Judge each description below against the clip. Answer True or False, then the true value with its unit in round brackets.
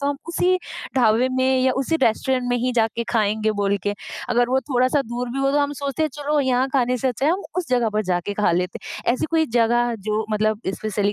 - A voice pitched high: True (245 Hz)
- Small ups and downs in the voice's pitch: False (3.8 semitones)